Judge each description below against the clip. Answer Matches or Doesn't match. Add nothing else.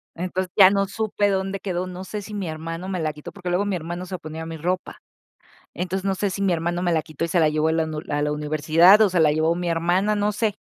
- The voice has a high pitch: Doesn't match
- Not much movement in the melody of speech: Doesn't match